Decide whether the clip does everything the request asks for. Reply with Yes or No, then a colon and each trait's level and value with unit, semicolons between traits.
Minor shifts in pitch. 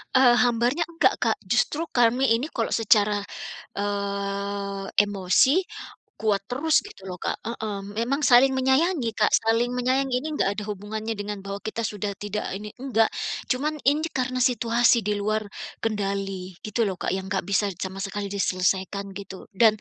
No: average, 3.9 semitones